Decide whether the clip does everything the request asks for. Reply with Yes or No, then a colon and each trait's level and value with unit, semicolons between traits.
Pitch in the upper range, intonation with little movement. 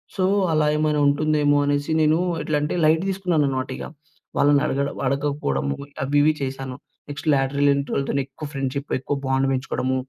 No: medium, 145 Hz; narrow, 2.0 semitones